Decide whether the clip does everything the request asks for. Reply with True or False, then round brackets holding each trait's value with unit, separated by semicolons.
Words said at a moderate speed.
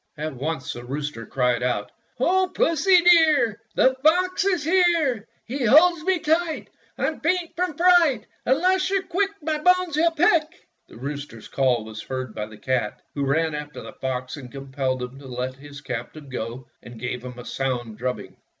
True (185 wpm)